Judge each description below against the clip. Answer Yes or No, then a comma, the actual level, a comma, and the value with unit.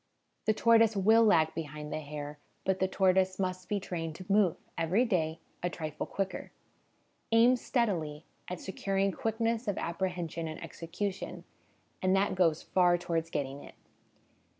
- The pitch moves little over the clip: No, average, 3.8 semitones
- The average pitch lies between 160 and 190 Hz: Yes, medium, 185 Hz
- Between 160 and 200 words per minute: No, average, 150 wpm